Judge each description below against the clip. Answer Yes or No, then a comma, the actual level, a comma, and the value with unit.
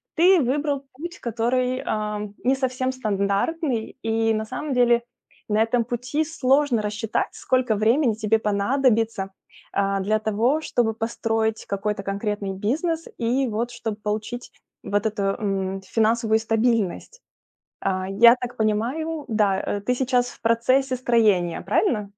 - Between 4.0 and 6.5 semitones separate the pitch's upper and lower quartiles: No, average, 3.4 semitones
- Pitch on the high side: Yes, high, 225 Hz